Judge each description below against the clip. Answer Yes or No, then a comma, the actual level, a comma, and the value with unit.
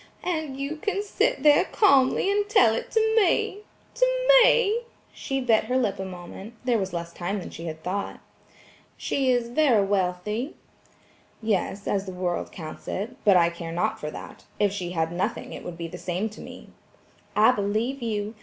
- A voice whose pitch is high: Yes, high, 215 Hz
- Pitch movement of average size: No, wide, 7.0 semitones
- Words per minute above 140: Yes, average, 180 wpm